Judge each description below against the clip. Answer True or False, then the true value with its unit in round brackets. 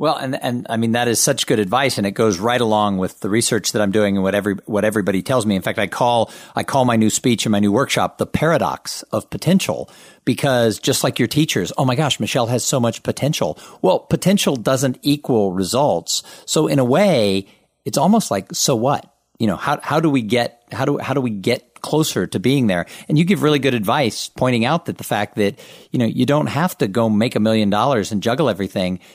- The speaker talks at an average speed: False (235 wpm)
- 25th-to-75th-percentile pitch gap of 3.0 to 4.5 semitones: False (4.9 semitones)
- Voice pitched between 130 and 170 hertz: False (120 Hz)